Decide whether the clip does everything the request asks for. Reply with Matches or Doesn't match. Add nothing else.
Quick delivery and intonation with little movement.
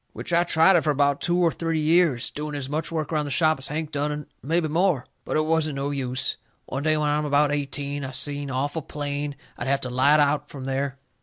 Matches